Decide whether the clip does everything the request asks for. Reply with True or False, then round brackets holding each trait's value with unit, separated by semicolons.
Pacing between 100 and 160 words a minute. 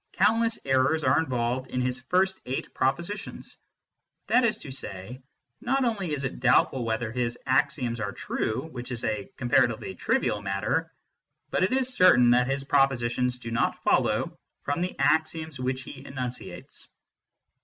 True (155 wpm)